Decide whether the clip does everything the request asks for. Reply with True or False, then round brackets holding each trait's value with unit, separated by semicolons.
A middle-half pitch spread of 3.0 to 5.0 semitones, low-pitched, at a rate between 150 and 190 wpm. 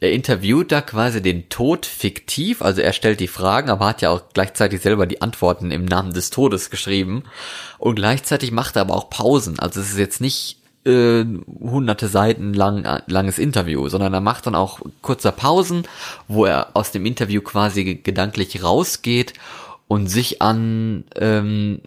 True (3.6 semitones; 105 Hz; 170 wpm)